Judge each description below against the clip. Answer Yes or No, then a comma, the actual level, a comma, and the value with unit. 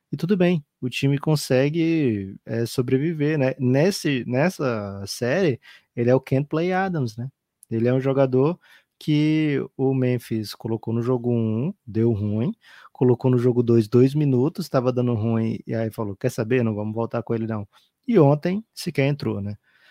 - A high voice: No, low, 130 Hz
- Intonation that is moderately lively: Yes, average, 4.3 semitones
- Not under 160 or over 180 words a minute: Yes, average, 175 wpm